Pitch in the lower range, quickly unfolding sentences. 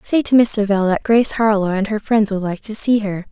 No: high, 210 Hz; fast, 270 wpm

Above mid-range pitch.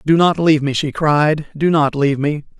No: medium, 150 Hz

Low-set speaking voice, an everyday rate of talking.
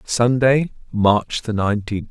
No: low, 115 Hz; slow, 85 wpm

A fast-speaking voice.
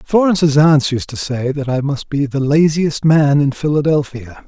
No: average, 190 wpm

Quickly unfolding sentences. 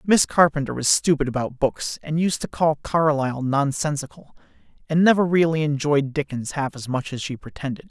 No: average, 175 wpm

